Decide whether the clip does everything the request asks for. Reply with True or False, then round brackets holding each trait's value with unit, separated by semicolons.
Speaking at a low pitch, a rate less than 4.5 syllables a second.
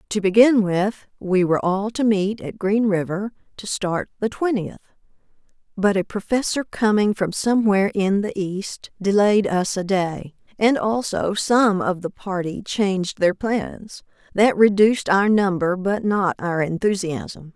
False (200 Hz; 4.2 syllables/s)